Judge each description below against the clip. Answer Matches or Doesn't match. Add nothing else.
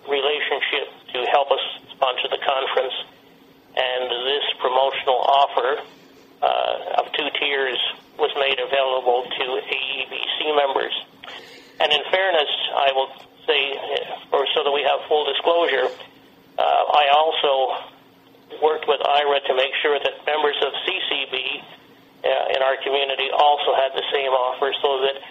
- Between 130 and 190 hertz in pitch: Matches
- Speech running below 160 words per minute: Matches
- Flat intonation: Matches